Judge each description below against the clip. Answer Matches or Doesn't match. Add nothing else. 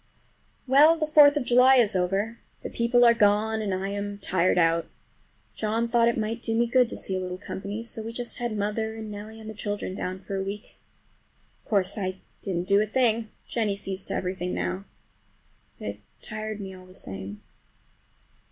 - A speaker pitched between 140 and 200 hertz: Doesn't match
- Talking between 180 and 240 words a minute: Matches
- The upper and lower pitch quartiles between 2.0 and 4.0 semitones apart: Matches